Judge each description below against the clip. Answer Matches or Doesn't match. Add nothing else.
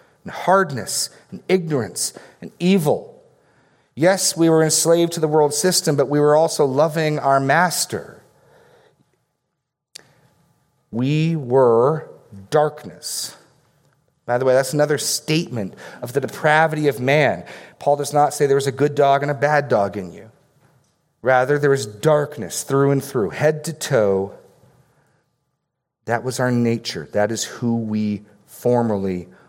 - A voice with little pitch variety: Doesn't match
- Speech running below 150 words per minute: Matches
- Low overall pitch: Doesn't match